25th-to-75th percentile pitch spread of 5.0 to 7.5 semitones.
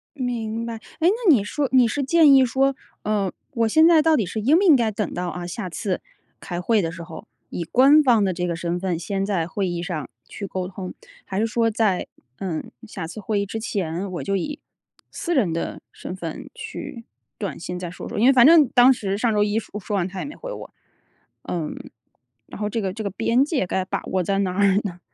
Yes: wide, 5.4 semitones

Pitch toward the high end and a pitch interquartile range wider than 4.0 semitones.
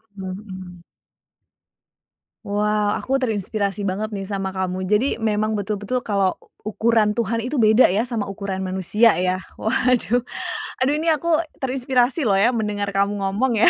No: high, 210 Hz; average, 3.2 semitones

